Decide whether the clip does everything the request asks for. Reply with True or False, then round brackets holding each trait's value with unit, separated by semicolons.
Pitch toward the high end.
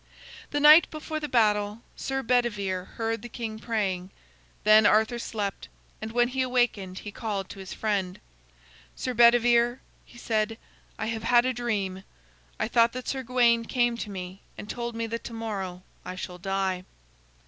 True (225 Hz)